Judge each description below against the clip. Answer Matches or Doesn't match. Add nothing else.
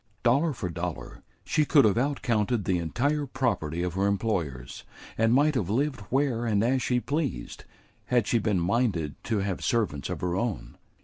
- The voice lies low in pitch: Matches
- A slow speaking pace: Doesn't match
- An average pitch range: Doesn't match